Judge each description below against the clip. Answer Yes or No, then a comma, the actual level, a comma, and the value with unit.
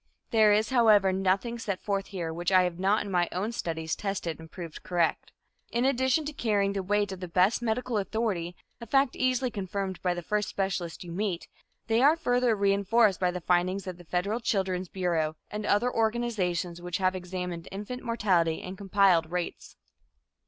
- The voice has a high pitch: Yes, high, 195 Hz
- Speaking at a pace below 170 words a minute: No, average, 185 wpm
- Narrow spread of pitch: No, average, 3.8 semitones